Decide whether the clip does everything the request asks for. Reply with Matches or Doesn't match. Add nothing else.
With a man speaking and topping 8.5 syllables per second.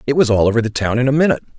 Matches